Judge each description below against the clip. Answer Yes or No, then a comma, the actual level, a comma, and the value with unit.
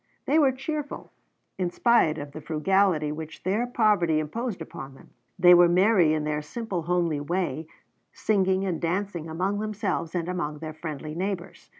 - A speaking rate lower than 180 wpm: Yes, average, 165 wpm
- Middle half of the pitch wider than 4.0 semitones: Yes, average, 4.4 semitones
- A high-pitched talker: No, medium, 175 Hz